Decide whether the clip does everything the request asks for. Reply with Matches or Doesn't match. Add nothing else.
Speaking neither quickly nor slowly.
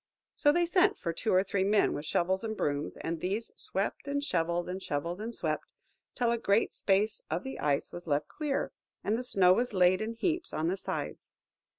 Doesn't match